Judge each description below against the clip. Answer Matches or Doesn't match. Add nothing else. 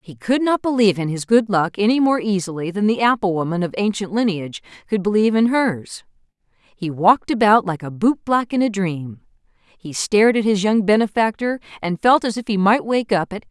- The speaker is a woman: Matches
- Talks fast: Matches